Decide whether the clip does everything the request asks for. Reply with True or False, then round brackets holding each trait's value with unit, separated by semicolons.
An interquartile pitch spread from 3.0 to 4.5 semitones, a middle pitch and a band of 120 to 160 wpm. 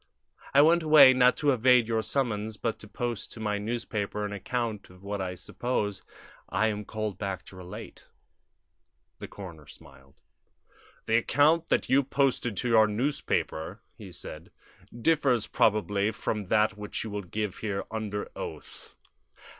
False (3.4 semitones; 110 Hz; 155 wpm)